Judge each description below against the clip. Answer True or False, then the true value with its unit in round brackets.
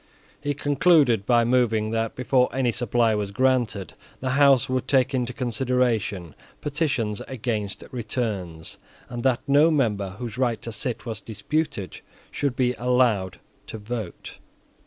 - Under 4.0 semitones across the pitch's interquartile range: True (3.3 semitones)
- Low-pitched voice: True (120 Hz)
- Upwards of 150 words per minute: False (135 wpm)